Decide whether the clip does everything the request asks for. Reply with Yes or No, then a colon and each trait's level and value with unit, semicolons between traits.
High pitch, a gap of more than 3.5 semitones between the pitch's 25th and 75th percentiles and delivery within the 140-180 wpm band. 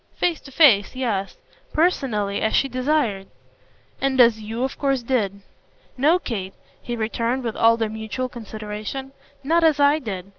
Yes: high, 240 Hz; average, 4.2 semitones; average, 155 wpm